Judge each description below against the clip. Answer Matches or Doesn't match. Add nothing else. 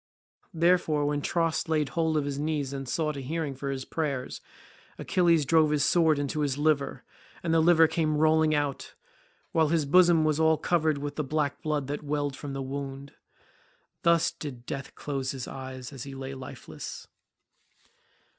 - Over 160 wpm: Matches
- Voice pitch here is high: Doesn't match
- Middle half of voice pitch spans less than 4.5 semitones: Matches